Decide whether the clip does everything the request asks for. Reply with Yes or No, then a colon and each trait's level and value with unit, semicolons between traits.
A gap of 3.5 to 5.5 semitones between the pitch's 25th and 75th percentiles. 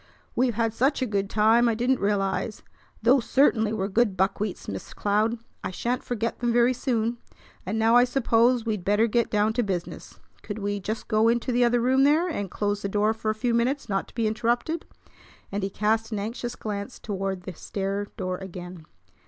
No: average, 2.9 semitones